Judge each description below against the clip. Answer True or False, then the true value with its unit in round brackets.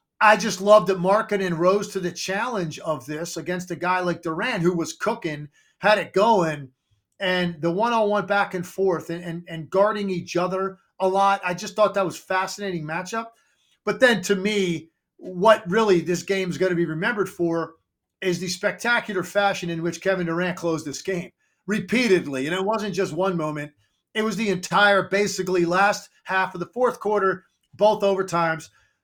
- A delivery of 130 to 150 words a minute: False (185 wpm)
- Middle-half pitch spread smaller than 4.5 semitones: True (3.0 semitones)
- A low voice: False (185 Hz)